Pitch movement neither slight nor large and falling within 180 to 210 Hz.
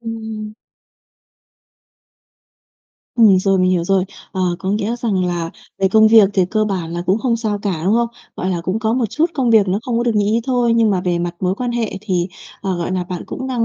Yes: average, 3.7 semitones; high, 205 Hz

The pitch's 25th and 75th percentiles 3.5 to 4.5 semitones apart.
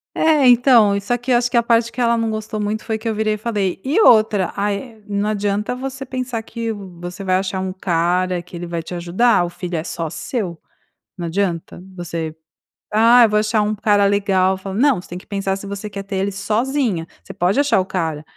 Yes: average, 3.8 semitones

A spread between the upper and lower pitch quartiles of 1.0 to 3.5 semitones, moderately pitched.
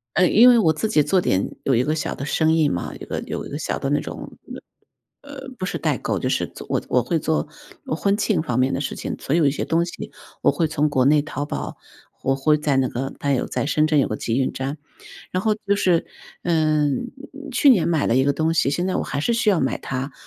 No: average, 4.0 semitones; medium, 155 Hz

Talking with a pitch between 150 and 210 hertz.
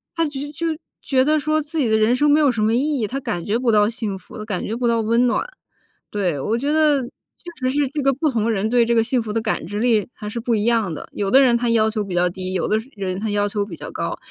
No: high, 230 Hz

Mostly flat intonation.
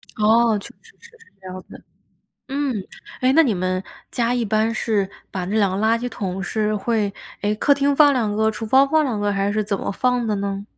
No: average, 3.6 semitones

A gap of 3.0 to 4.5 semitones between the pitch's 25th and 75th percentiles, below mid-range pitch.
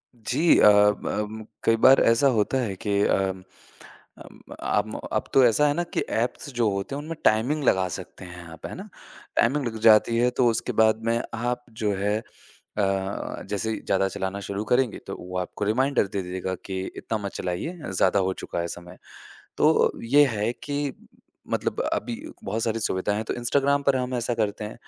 Yes: average, 4.0 semitones; low, 110 Hz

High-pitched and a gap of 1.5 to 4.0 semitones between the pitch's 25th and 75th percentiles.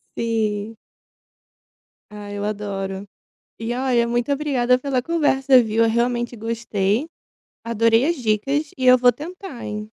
Yes: high, 235 Hz; average, 3.6 semitones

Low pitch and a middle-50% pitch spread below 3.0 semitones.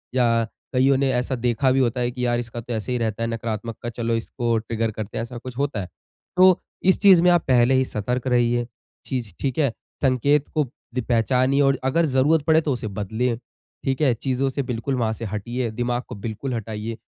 Yes: low, 125 Hz; narrow, 2.6 semitones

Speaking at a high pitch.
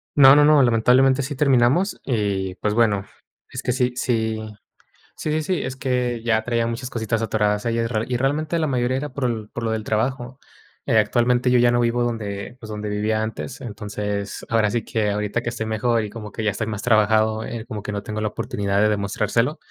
No: low, 115 Hz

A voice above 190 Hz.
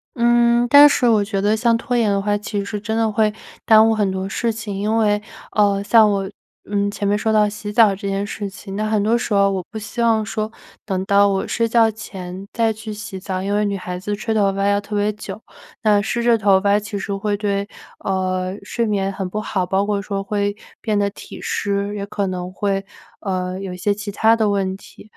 Yes: high, 205 Hz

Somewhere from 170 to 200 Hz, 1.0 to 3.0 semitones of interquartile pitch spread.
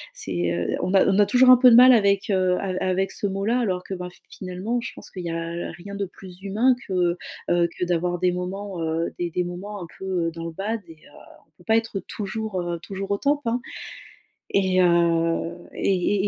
Yes: medium, 185 Hz; average, 2.7 semitones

